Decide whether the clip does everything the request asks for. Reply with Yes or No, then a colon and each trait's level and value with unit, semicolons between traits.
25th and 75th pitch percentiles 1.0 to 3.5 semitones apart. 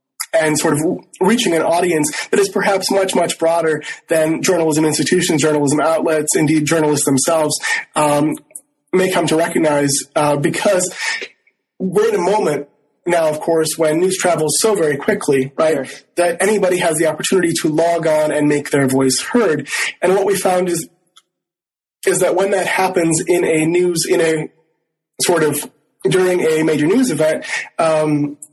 Yes: average, 3.2 semitones